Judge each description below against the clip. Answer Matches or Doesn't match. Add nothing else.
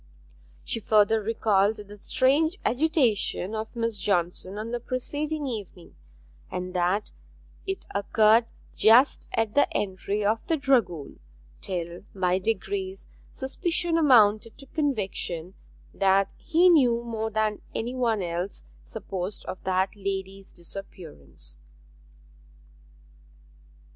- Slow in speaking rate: Matches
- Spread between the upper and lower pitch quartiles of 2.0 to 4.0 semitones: Doesn't match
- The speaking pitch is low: Doesn't match